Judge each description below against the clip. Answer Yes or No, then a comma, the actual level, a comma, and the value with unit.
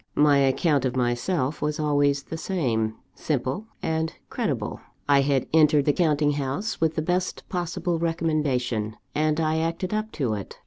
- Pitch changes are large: No, average, 3.2 semitones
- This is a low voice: No, medium, 150 Hz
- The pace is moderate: Yes, average, 155 wpm